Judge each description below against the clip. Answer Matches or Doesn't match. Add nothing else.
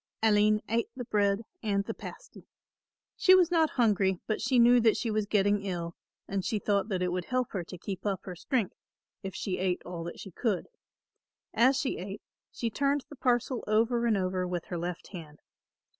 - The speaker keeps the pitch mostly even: Doesn't match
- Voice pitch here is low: Doesn't match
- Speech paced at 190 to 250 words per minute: Matches